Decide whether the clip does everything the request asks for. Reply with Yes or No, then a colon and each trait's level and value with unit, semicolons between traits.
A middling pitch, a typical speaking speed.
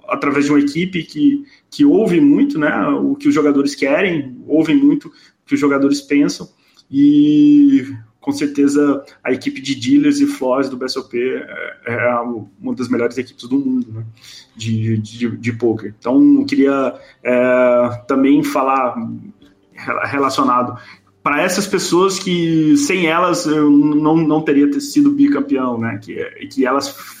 Yes: medium, 150 Hz; average, 155 wpm